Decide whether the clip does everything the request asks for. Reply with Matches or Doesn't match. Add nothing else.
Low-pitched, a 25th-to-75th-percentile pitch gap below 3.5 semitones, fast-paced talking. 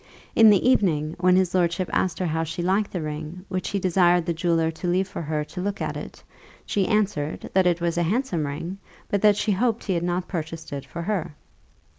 Doesn't match